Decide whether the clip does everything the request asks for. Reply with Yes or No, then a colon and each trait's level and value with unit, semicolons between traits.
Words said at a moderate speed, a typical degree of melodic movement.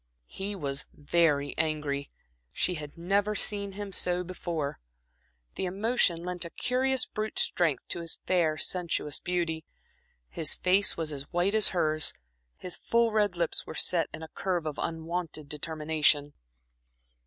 Yes: average, 145 wpm; average, 3.7 semitones